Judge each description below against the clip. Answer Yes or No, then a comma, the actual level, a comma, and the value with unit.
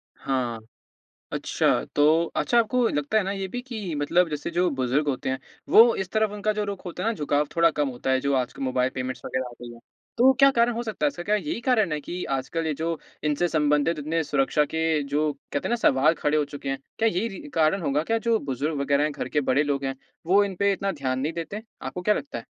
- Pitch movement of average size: No, wide, 6.5 semitones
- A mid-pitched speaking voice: Yes, medium, 160 Hz